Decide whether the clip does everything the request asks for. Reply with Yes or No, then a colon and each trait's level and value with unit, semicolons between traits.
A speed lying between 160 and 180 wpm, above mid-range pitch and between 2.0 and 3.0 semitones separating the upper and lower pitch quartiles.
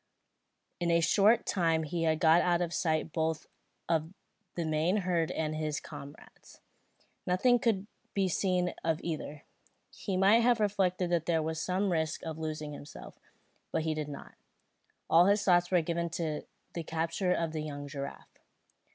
No: average, 165 wpm; medium, 165 Hz; narrow, 2.5 semitones